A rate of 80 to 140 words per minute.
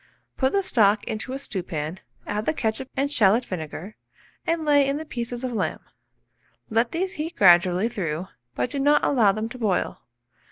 No: average, 175 wpm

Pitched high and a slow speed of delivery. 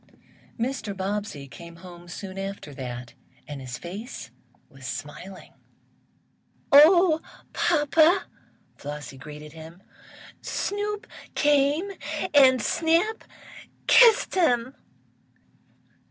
Yes: high, 205 Hz; slow, 80 wpm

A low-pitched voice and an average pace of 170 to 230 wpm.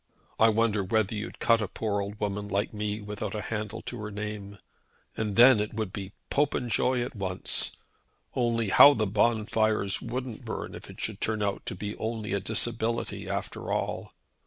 Yes: low, 105 Hz; average, 180 wpm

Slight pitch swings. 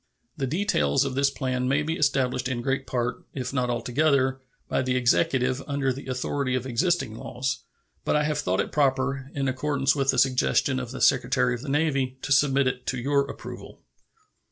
Yes: narrow, 1.6 semitones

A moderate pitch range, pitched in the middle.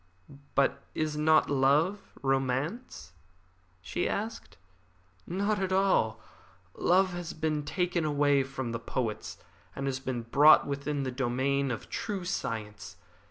Yes: average, 5.0 semitones; medium, 145 Hz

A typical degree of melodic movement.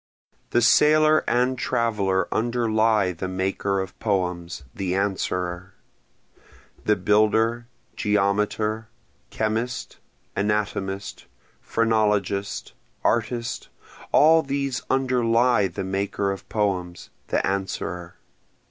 Yes: average, 3.5 semitones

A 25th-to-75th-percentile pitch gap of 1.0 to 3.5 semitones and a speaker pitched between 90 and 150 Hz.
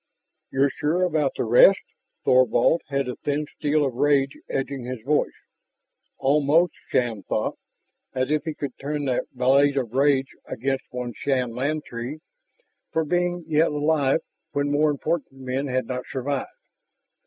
Yes: average, 2.7 semitones; medium, 140 Hz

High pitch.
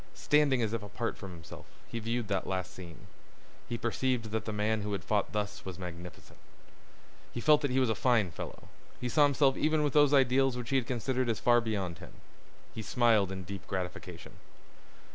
No: low, 115 Hz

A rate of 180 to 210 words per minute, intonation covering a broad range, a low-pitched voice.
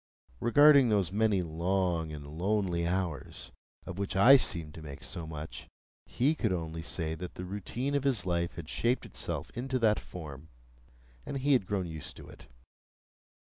No: average, 170 wpm; wide, 5.8 semitones; very low, 90 Hz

